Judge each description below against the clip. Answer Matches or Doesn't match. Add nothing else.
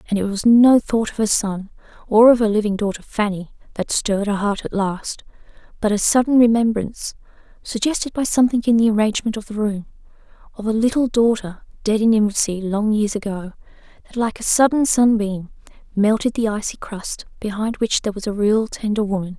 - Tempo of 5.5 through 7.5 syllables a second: Matches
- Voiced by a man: Doesn't match